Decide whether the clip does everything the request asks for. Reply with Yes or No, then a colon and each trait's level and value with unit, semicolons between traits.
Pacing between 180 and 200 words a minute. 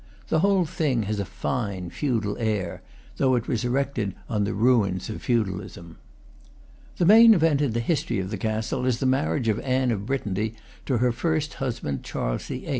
Yes: average, 185 wpm